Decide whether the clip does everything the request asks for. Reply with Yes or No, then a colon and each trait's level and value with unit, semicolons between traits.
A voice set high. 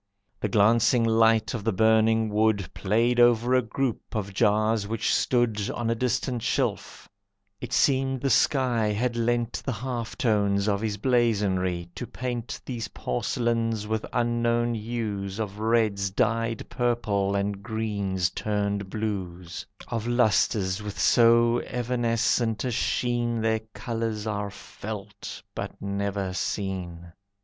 No: low, 110 Hz